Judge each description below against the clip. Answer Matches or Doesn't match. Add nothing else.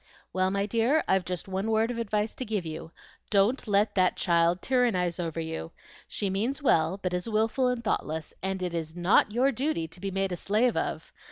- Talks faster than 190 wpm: Matches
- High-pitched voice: Matches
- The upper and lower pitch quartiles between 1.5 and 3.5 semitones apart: Doesn't match